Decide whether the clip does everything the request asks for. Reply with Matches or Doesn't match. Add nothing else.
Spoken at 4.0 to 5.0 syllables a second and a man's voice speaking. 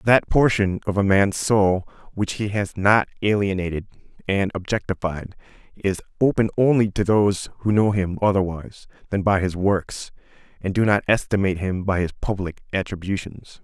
Doesn't match